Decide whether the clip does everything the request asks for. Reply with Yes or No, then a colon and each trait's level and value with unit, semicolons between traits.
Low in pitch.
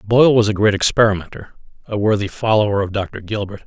Yes: low, 105 Hz